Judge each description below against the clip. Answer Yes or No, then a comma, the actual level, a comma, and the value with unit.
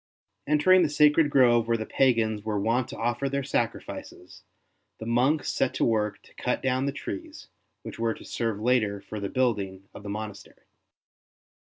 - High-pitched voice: No, low, 115 Hz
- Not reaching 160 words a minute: No, average, 175 wpm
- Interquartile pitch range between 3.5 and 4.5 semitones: Yes, average, 4.0 semitones